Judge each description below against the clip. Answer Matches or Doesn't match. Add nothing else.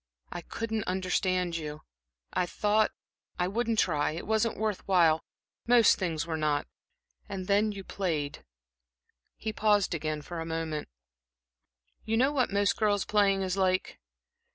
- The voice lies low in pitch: Doesn't match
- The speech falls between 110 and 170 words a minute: Matches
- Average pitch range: Matches